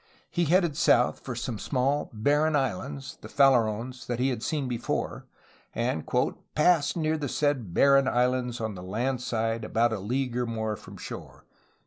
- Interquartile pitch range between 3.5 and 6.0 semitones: Yes, average, 3.8 semitones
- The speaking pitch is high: No, low, 125 Hz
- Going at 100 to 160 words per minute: No, average, 170 wpm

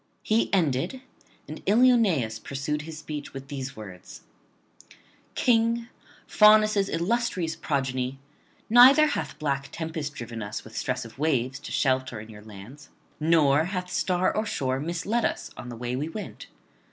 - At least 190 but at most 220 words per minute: No, average, 145 wpm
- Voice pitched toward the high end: No, medium, 150 Hz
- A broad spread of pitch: Yes, wide, 7.3 semitones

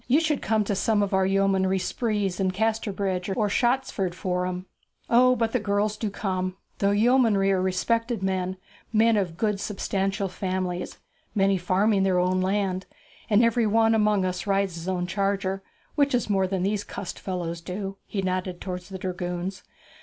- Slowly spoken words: No, average, 170 wpm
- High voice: Yes, high, 195 Hz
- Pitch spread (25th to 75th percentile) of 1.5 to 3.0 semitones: Yes, narrow, 2.4 semitones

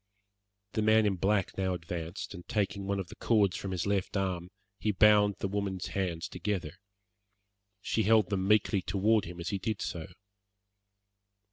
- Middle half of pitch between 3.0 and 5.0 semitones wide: No, narrow, 2.4 semitones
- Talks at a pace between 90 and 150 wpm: No, average, 165 wpm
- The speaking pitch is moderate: No, very low, 95 Hz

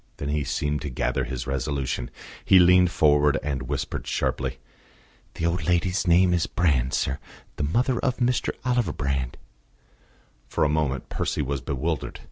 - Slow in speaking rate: No, average, 155 wpm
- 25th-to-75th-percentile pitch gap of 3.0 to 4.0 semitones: No, average, 4.5 semitones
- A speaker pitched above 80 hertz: No, very low, 75 Hz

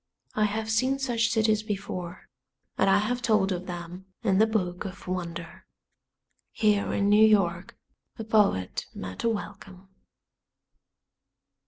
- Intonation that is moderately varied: Yes, average, 3.1 semitones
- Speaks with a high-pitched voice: Yes, high, 205 Hz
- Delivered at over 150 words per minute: No, slow, 135 wpm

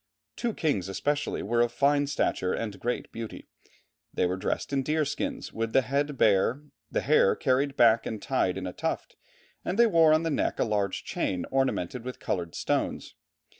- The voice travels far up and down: Yes, wide, 6.0 semitones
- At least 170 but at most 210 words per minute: Yes, average, 185 wpm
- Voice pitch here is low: Yes, low, 130 Hz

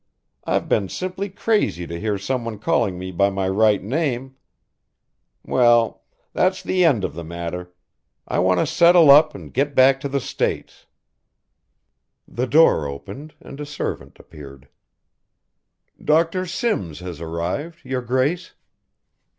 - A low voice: Yes, low, 125 Hz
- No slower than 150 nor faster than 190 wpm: No, average, 140 wpm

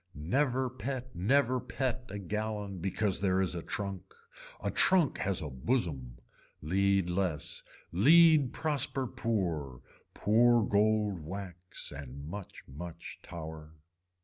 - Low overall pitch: Yes, low, 100 Hz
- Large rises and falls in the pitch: Yes, wide, 6.1 semitones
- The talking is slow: Yes, slow, 120 wpm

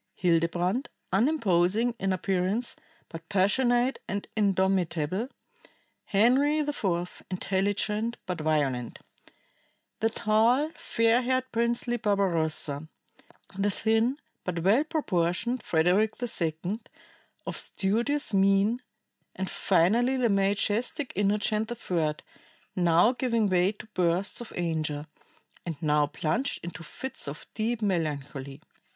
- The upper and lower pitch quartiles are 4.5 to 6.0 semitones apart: Yes, average, 5.3 semitones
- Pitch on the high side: Yes, high, 195 Hz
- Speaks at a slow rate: Yes, slow, 105 wpm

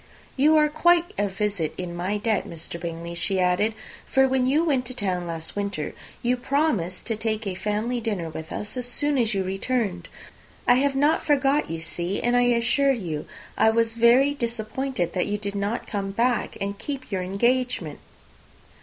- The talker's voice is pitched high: Yes, high, 220 Hz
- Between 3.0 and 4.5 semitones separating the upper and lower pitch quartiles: No, wide, 5.4 semitones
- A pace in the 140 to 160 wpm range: No, average, 190 wpm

